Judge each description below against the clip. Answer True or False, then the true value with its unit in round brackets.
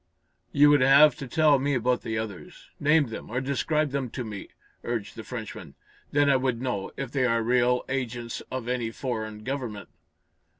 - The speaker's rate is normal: True (180 wpm)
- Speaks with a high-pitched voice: False (125 Hz)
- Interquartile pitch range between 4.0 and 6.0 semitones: False (3.2 semitones)